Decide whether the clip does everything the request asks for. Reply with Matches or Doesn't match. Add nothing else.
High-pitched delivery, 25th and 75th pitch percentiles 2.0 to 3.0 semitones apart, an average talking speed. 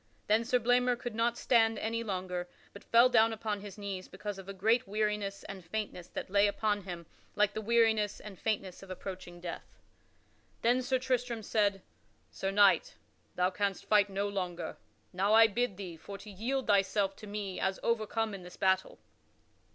Matches